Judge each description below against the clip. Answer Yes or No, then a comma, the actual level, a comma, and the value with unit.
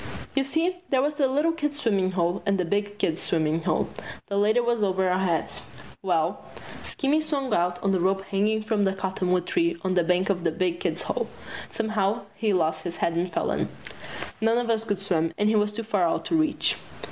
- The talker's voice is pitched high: Yes, high, 200 Hz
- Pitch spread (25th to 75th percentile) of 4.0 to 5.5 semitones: Yes, average, 4.4 semitones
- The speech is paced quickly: Yes, fast, 215 wpm